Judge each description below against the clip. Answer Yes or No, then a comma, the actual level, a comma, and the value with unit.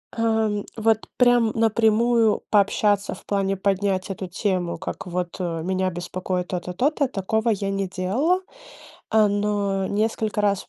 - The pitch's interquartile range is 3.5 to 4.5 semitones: No, average, 2.9 semitones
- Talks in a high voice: Yes, high, 205 Hz